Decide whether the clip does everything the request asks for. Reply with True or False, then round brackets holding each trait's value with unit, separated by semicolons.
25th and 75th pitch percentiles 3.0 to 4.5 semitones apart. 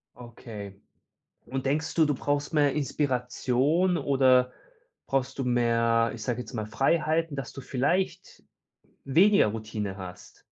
True (4.1 semitones)